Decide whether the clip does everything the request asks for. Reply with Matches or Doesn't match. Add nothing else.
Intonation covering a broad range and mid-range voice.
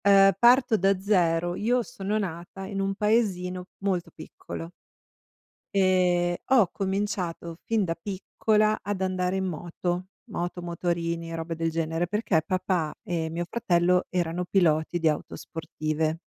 Doesn't match